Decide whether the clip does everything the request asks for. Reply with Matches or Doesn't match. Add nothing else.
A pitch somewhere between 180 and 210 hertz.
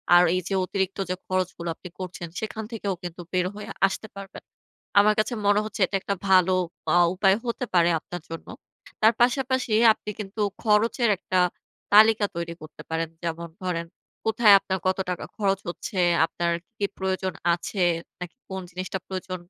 Matches